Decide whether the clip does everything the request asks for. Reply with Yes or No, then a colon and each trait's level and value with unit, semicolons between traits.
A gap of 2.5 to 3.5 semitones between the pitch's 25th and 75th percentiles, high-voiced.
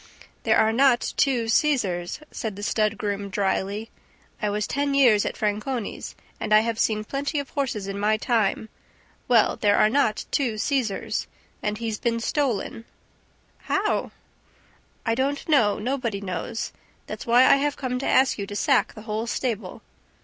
No: average, 4.1 semitones; high, 225 Hz